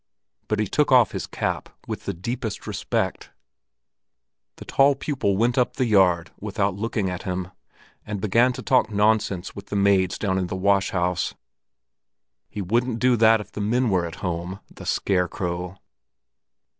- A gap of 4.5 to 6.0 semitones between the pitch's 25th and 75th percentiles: No, average, 3.9 semitones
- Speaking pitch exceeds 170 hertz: No, low, 100 Hz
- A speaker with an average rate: Yes, average, 165 wpm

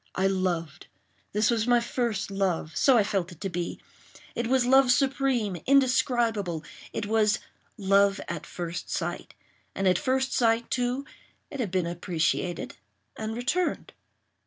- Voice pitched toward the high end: Yes, high, 215 Hz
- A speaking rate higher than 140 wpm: No, slow, 135 wpm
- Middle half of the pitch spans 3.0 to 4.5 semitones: No, average, 5.1 semitones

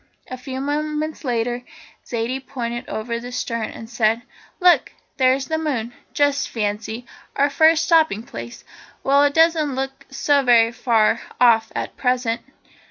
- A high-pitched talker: Yes, very high, 255 Hz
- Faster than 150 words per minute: No, average, 145 wpm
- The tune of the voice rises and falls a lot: No, average, 3.7 semitones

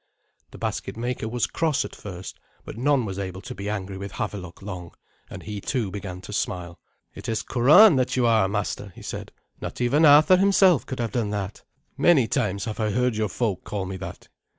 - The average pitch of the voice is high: No, low, 110 Hz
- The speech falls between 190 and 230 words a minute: Yes, fast, 205 wpm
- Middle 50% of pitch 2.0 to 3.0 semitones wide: No, average, 4.4 semitones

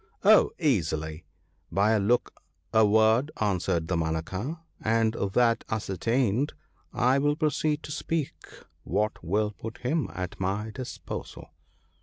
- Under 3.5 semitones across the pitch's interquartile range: No, average, 5.2 semitones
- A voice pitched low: Yes, low, 110 Hz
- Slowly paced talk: Yes, slow, 130 wpm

